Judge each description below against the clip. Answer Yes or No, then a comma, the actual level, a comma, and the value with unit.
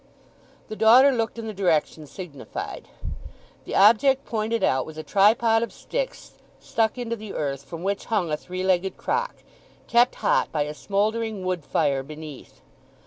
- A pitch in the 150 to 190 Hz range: No, high, 200 Hz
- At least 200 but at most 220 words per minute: No, average, 160 wpm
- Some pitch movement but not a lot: No, wide, 6.3 semitones